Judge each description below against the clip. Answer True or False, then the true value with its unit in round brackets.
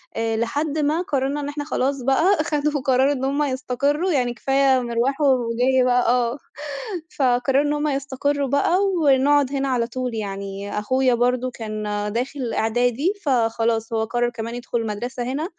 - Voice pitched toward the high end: True (260 Hz)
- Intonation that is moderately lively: True (3.0 semitones)